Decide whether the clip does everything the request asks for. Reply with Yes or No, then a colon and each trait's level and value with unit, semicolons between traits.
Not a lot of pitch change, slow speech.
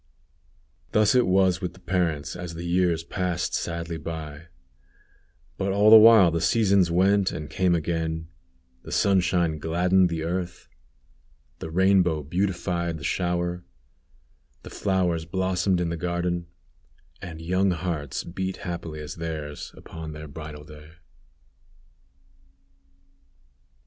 Yes: narrow, 2.3 semitones; slow, 125 wpm